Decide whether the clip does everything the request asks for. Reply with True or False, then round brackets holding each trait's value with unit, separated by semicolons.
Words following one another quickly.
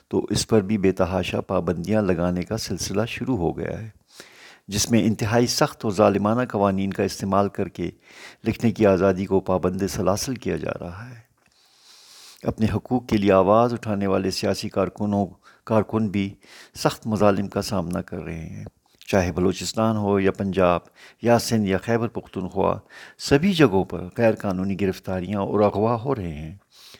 False (165 wpm)